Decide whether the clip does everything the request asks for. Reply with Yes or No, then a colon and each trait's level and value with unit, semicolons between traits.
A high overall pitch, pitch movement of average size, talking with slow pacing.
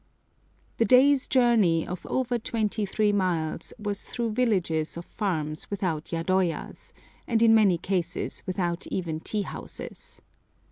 Yes: high, 195 Hz; average, 4.7 semitones; slow, 130 wpm